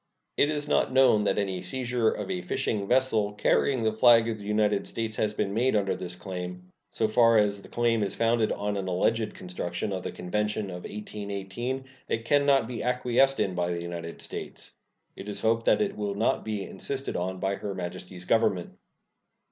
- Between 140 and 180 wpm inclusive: No, average, 195 wpm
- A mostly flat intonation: No, average, 3.6 semitones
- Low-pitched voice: Yes, low, 105 Hz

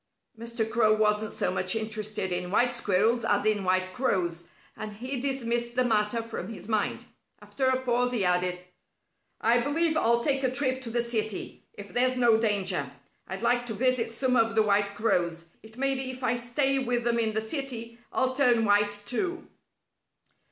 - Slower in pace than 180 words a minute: No, average, 185 wpm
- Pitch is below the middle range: No, high, 230 Hz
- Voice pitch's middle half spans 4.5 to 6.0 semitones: No, average, 3.2 semitones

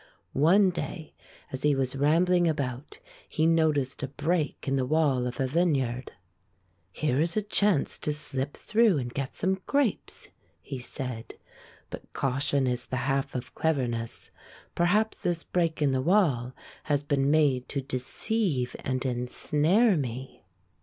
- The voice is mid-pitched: Yes, medium, 145 Hz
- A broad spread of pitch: No, average, 4.4 semitones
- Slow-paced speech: No, average, 155 wpm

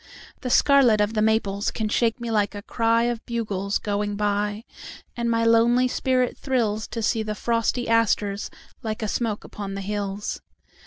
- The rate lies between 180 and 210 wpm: No, average, 155 wpm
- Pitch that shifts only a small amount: Yes, narrow, 2.2 semitones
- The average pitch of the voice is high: Yes, high, 220 Hz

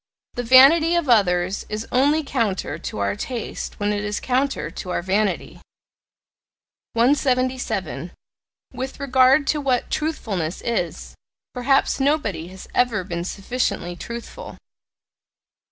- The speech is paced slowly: Yes, slow, 120 wpm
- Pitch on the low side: No, high, 240 Hz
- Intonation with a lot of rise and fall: Yes, wide, 6.0 semitones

